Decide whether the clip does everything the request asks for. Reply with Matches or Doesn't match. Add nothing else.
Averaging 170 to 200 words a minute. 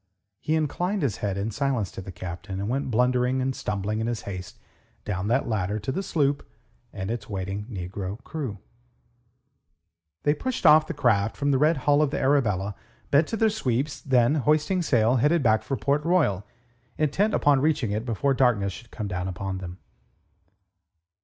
Matches